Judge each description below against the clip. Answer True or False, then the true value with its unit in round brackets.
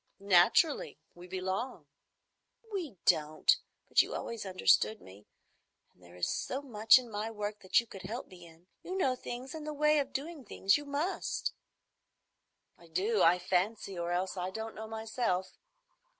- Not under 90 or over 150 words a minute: False (165 wpm)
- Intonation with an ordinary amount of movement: False (6.0 semitones)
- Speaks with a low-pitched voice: False (210 Hz)